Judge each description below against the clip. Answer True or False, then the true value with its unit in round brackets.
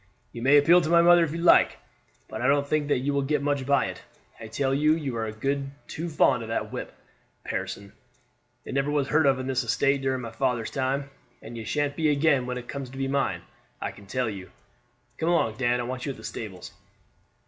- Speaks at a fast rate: True (235 wpm)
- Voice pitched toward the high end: False (135 Hz)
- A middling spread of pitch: True (3.0 semitones)